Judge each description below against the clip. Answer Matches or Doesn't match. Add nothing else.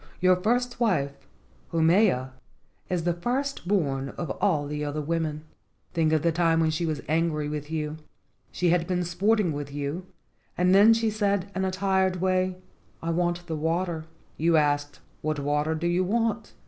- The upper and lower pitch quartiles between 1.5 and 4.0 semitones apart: Matches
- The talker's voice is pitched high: Doesn't match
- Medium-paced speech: Matches